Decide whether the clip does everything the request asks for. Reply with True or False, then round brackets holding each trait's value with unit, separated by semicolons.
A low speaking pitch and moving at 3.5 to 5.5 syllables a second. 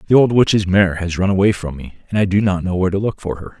False (95 Hz; 6.4 syllables/s)